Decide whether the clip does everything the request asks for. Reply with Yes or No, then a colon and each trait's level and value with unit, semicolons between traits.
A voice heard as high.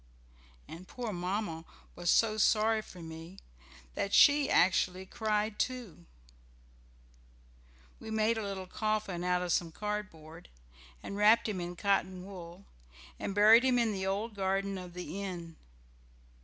Yes: high, 195 Hz